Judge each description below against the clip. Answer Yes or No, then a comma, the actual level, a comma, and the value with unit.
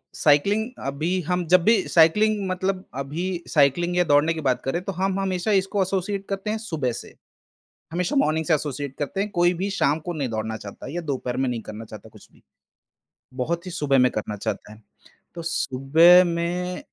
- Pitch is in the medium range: Yes, medium, 170 Hz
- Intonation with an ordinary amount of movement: Yes, average, 5.0 semitones